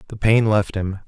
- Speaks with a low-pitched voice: Yes, low, 105 Hz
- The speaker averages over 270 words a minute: No, fast, 225 wpm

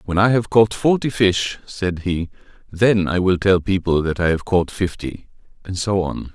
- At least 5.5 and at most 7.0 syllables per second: No, 4.5 syllables/s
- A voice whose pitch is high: No, very low, 95 Hz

